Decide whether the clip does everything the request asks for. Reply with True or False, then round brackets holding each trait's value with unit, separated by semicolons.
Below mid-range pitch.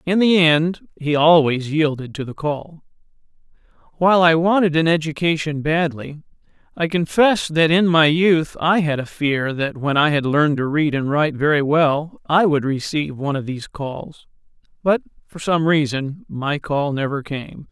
False (155 Hz)